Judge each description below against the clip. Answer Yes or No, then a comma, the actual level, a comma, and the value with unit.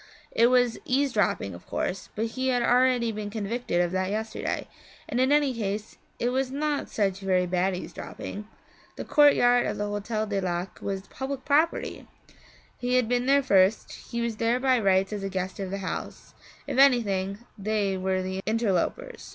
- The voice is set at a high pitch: Yes, high, 220 Hz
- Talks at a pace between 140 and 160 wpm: No, average, 175 wpm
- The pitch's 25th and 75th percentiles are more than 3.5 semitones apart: Yes, average, 4.6 semitones